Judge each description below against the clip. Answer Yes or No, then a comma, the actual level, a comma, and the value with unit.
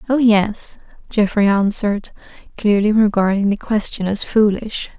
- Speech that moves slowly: Yes, slow, 120 wpm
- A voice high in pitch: Yes, high, 210 Hz